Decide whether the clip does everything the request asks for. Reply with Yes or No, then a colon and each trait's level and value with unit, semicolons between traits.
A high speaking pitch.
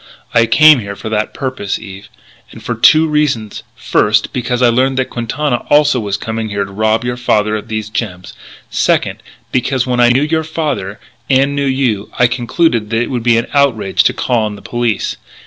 No: low, 120 Hz